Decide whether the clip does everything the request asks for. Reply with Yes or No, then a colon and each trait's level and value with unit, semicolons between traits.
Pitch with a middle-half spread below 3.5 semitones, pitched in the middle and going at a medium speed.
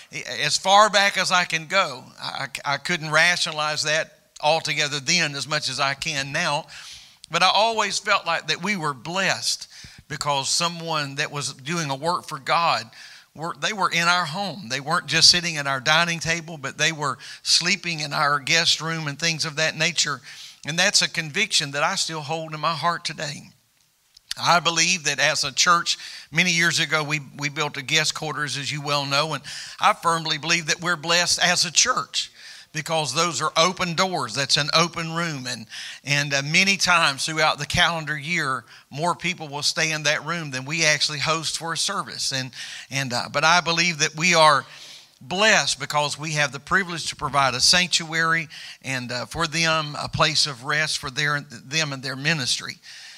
Yes: average, 2.7 semitones; medium, 160 Hz; average, 190 wpm